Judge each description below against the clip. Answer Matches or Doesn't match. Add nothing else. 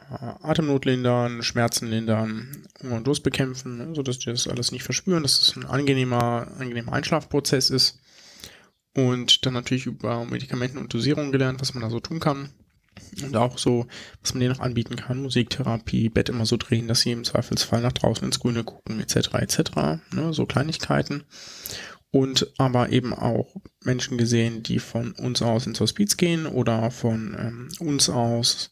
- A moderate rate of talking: Matches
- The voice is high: Doesn't match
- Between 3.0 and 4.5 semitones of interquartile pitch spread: Doesn't match